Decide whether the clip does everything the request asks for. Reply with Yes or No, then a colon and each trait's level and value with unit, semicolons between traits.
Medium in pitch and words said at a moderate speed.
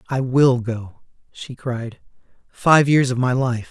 No: low, 125 Hz; average, 160 wpm